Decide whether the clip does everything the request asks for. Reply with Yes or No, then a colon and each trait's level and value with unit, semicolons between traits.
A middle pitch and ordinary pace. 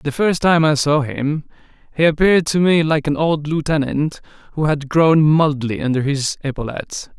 Yes: medium, 150 Hz; average, 175 wpm